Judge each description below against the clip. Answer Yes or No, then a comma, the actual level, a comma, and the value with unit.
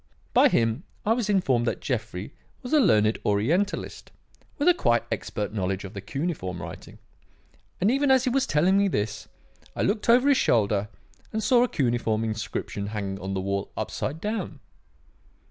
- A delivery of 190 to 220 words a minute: No, average, 170 wpm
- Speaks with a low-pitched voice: Yes, low, 120 Hz